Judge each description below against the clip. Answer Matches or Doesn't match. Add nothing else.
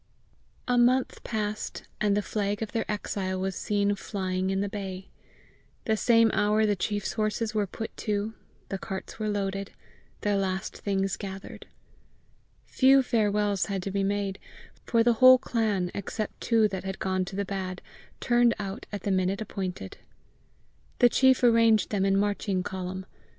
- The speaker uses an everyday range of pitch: Doesn't match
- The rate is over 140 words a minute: Matches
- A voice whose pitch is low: Doesn't match